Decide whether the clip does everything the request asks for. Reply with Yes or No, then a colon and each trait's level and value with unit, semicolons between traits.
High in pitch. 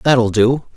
No: low, 120 Hz